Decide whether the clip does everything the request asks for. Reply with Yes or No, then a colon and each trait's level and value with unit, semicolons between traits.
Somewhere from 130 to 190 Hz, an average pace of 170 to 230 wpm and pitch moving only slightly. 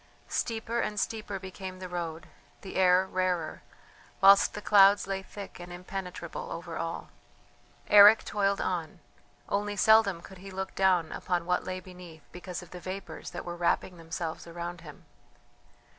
No: medium, 185 Hz; average, 155 wpm; narrow, 2.2 semitones